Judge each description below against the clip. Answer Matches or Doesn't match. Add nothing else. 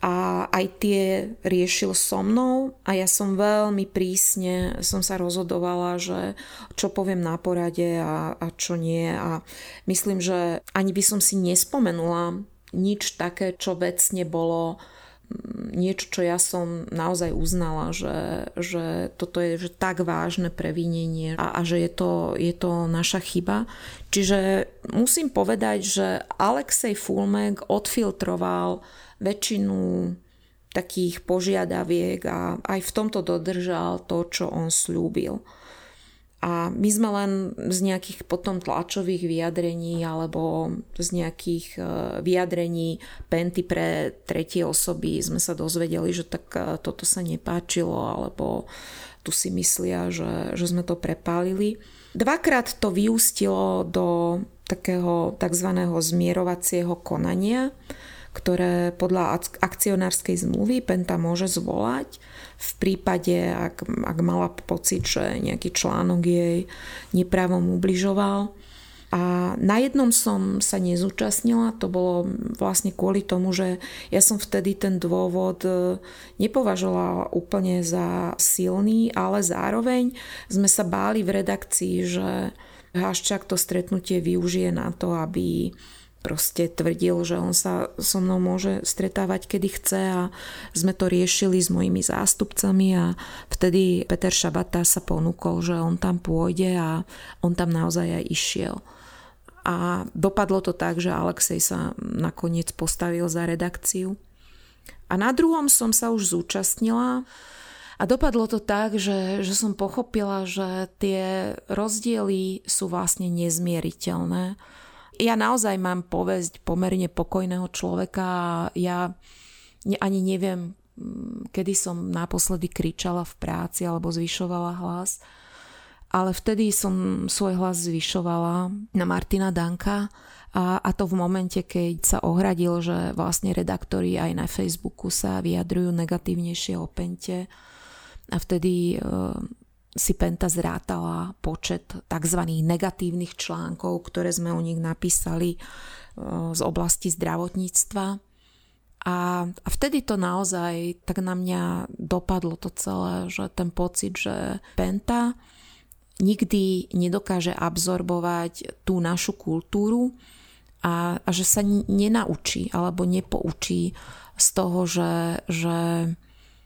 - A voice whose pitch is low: Doesn't match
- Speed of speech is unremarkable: Matches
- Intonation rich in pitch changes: Doesn't match